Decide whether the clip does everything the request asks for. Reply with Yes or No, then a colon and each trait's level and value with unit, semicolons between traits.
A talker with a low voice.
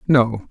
Yes: low, 125 Hz